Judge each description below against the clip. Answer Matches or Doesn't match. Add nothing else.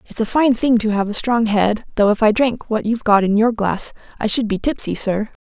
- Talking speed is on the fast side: Matches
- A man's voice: Doesn't match